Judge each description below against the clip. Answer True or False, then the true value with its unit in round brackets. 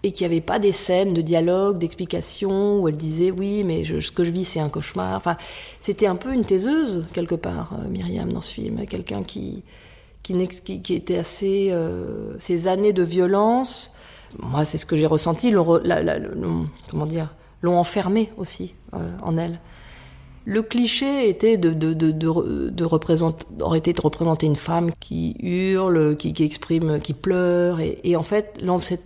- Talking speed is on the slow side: False (180 wpm)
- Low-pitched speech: False (175 Hz)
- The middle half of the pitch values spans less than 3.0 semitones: False (3.3 semitones)